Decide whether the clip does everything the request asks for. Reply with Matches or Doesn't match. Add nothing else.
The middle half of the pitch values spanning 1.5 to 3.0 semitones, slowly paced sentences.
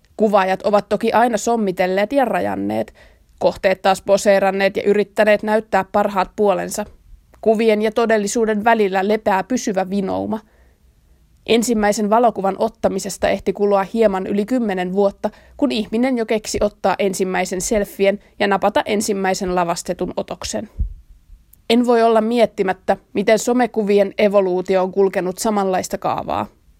Doesn't match